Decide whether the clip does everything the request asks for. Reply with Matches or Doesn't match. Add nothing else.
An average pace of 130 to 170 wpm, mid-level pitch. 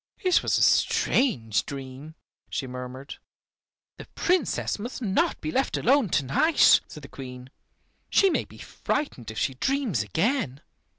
Matches